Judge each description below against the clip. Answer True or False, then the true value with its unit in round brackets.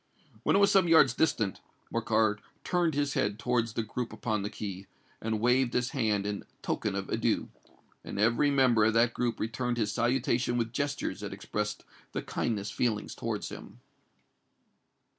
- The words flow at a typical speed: True (160 wpm)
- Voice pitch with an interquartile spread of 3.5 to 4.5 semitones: False (3.0 semitones)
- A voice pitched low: True (115 Hz)